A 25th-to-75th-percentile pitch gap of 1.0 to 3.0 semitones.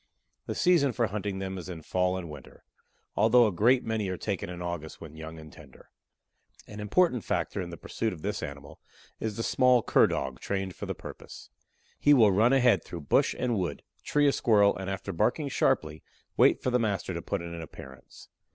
No: average, 5.2 semitones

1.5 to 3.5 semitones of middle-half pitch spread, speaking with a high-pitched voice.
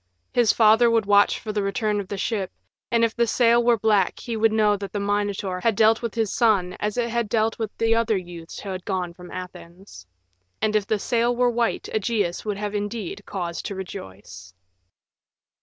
Yes: average, 2.9 semitones; high, 210 Hz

